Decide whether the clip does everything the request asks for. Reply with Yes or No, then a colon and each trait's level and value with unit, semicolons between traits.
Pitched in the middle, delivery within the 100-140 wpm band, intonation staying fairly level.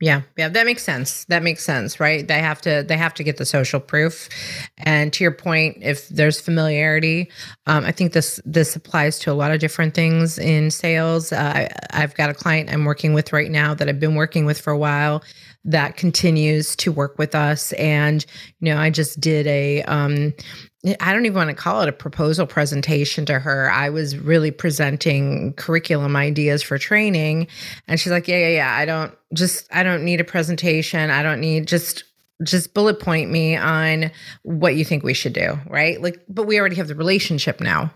No: medium, 155 Hz; fast, 205 wpm; narrow, 1.9 semitones